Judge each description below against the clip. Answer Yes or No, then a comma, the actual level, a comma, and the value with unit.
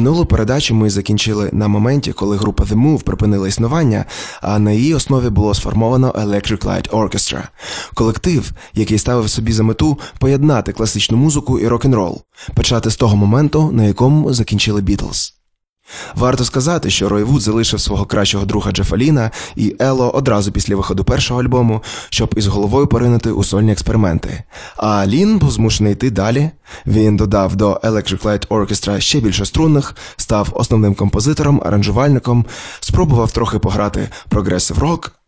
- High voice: No, low, 110 Hz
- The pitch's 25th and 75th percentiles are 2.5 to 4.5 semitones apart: Yes, average, 3.6 semitones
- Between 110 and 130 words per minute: No, average, 150 wpm